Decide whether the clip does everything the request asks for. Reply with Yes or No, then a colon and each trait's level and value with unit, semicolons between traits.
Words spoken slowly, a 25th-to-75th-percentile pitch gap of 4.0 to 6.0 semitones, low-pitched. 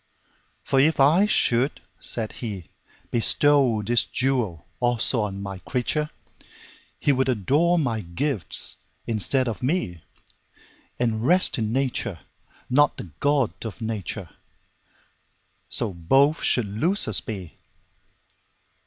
Yes: slow, 100 wpm; average, 5.1 semitones; low, 120 Hz